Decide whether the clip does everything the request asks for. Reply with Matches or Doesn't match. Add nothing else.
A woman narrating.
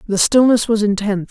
Matches